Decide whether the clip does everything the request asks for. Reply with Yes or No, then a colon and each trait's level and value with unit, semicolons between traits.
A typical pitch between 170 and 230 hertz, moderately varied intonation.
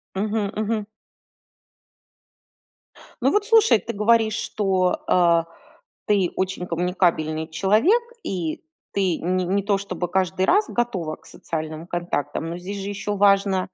Yes: high, 190 Hz; average, 3.2 semitones